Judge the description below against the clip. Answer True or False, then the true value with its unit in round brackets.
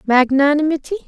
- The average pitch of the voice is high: True (295 Hz)